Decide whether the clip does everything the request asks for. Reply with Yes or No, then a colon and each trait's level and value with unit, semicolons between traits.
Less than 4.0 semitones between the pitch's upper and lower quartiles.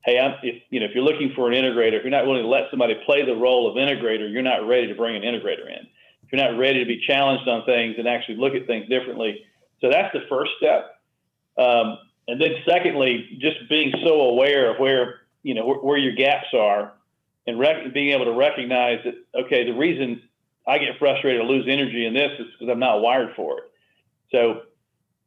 Yes: average, 2.8 semitones